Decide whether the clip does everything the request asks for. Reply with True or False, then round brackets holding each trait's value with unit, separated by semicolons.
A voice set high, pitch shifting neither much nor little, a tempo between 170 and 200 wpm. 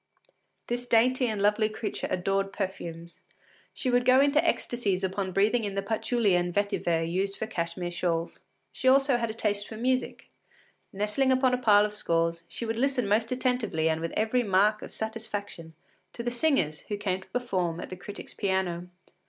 True (210 Hz; 4.7 semitones; 180 wpm)